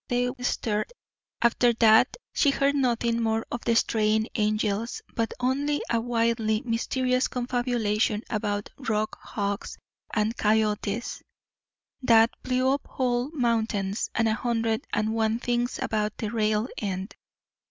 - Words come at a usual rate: No, slow, 130 wpm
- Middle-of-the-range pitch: No, high, 230 Hz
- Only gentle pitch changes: Yes, narrow, 2.3 semitones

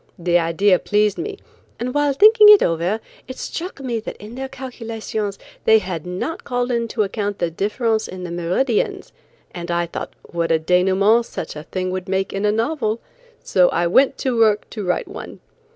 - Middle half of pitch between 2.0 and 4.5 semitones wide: No, average, 5.3 semitones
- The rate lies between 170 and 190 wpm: Yes, average, 185 wpm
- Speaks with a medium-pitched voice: No, high, 210 Hz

